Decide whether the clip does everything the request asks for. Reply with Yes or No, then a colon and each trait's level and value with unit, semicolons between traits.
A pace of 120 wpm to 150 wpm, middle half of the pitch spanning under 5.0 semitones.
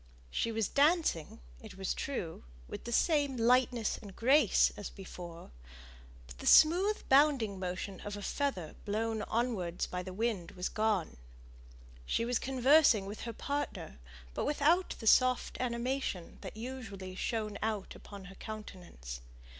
No: average, 145 wpm; wide, 5.5 semitones